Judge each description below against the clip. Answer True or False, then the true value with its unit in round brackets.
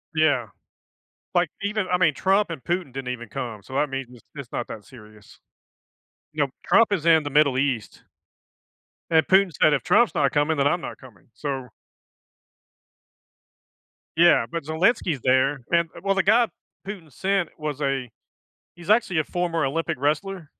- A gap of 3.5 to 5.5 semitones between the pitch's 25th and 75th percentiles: True (4.9 semitones)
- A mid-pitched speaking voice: True (155 Hz)